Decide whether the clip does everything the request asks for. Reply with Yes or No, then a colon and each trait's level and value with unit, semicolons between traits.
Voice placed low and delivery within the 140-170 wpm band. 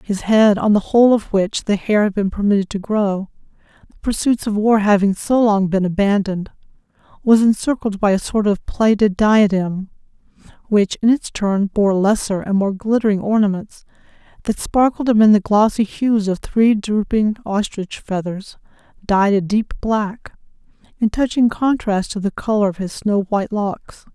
No: high, 210 Hz; average, 165 wpm